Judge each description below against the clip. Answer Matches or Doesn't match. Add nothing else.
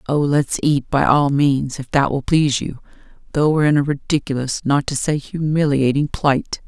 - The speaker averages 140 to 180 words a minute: Doesn't match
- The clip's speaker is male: Doesn't match